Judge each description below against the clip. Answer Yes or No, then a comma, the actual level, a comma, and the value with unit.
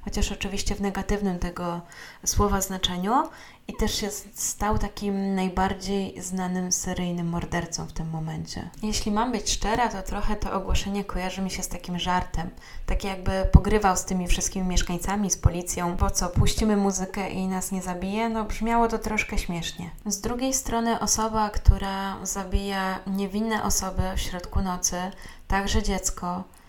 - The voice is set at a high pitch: Yes, high, 195 Hz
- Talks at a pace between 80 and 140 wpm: No, average, 155 wpm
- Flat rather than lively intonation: Yes, narrow, 2.3 semitones